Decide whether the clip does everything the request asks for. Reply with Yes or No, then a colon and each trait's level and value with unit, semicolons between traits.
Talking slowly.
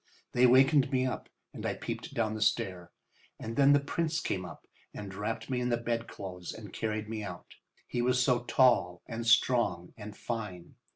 No: average, 185 wpm